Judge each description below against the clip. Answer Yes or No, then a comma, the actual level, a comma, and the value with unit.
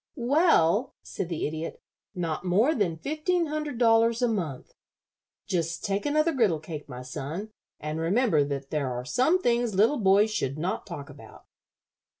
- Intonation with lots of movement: Yes, wide, 7.6 semitones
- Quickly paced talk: No, average, 155 wpm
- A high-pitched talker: Yes, high, 195 Hz